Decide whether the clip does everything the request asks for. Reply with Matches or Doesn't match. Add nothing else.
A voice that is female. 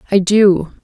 Matches